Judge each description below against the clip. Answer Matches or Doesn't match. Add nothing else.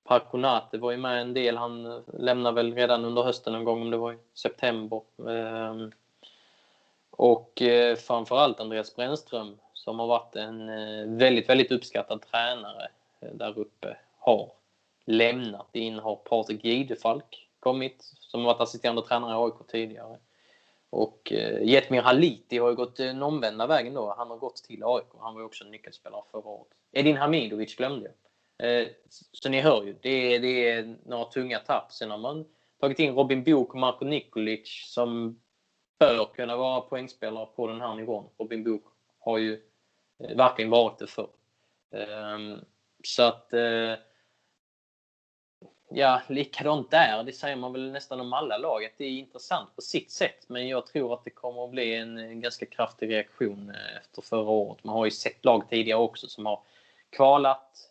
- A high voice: Doesn't match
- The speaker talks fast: Doesn't match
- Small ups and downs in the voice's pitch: Matches